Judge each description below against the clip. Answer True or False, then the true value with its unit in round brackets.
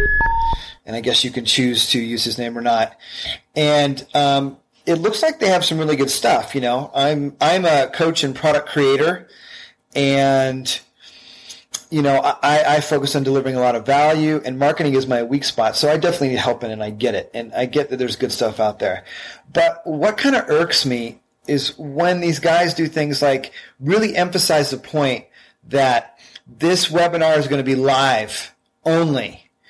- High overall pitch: False (140 Hz)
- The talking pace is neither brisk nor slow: True (190 wpm)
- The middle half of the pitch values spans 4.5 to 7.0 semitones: False (4.0 semitones)